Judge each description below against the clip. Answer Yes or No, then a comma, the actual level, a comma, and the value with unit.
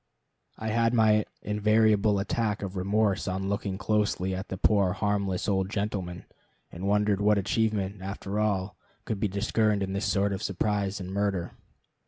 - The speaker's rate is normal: Yes, average, 160 wpm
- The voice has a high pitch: No, low, 100 Hz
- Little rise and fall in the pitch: Yes, narrow, 1.8 semitones